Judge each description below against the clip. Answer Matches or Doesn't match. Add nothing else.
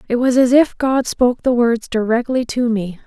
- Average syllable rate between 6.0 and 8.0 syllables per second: Doesn't match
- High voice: Matches